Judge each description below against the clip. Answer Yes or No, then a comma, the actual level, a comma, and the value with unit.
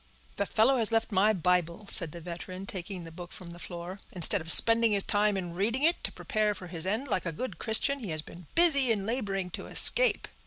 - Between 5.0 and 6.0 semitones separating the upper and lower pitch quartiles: No, average, 4.4 semitones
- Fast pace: Yes, fast, 230 wpm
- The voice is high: Yes, high, 195 Hz